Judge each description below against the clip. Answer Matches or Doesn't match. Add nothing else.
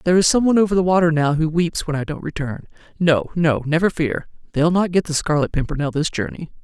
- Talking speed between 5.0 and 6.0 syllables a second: Doesn't match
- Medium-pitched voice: Matches